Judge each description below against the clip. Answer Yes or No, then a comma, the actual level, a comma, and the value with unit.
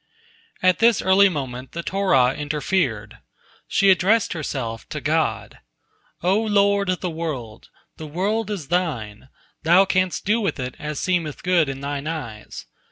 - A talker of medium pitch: Yes, medium, 170 Hz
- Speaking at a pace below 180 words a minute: Yes, average, 150 wpm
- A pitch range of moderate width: No, wide, 5.8 semitones